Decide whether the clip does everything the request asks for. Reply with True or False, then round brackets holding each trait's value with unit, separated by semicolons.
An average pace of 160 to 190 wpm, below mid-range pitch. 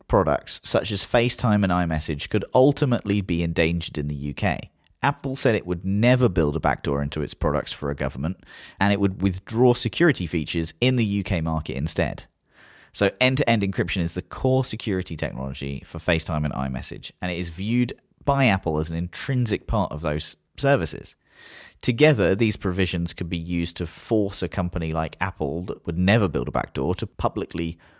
True (180 wpm; 90 Hz)